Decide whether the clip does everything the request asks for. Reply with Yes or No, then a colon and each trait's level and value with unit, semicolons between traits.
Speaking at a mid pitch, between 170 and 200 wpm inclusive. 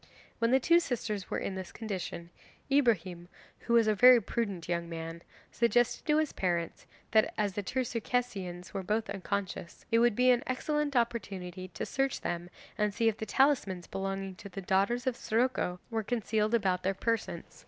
No: high, 210 Hz; average, 180 wpm